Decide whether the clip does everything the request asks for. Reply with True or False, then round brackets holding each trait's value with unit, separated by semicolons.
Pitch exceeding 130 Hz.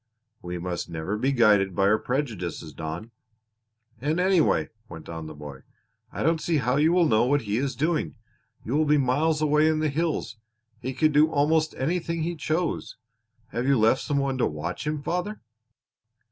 True (140 Hz)